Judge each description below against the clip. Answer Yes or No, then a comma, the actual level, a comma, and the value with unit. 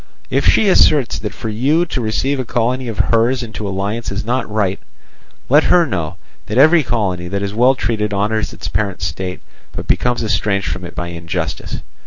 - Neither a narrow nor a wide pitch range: Yes, average, 4.4 semitones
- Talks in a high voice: No, low, 110 Hz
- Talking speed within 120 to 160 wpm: No, average, 190 wpm